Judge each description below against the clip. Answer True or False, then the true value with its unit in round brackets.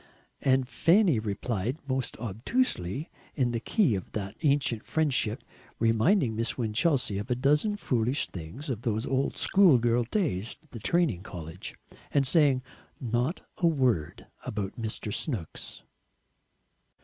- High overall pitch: False (120 Hz)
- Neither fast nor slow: False (130 wpm)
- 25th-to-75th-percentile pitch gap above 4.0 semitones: True (5.1 semitones)